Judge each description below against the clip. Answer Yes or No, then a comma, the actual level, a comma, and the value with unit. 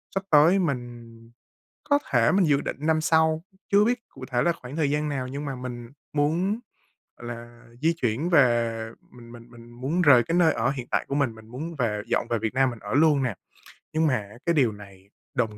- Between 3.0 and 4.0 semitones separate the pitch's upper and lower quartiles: No, average, 5.1 semitones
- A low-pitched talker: Yes, low, 130 Hz